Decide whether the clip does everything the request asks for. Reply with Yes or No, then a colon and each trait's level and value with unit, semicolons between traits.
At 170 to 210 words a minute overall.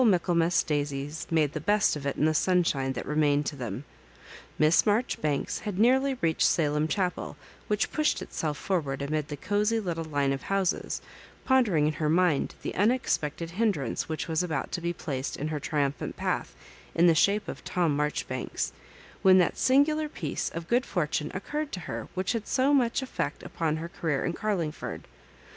Yes: average, 175 wpm